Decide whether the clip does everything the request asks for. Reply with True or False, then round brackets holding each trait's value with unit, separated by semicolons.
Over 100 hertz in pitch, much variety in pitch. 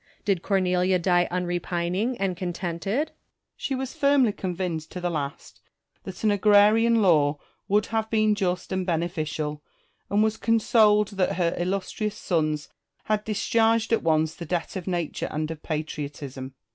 False (185 Hz; 4.1 semitones)